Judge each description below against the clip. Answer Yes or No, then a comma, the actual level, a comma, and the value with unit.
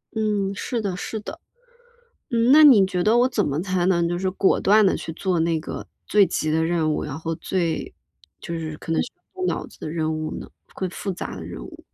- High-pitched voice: No, medium, 180 Hz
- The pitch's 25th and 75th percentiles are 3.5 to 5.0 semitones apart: Yes, average, 4.5 semitones